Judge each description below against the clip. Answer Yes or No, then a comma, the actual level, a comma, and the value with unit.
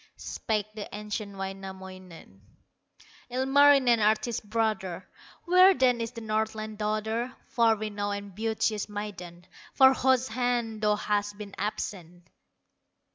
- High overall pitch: Yes, high, 215 Hz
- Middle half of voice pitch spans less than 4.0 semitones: Yes, narrow, 2.6 semitones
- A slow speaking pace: Yes, slow, 115 wpm